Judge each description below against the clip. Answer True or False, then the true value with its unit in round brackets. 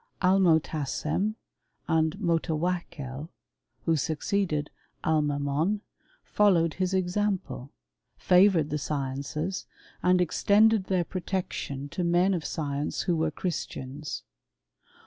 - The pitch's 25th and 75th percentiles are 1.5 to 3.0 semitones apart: False (3.8 semitones)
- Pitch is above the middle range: False (165 Hz)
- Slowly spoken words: True (95 wpm)